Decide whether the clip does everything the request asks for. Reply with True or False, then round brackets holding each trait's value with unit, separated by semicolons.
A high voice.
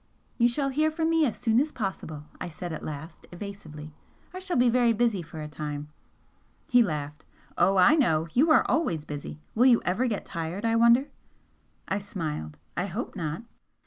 True (195 Hz)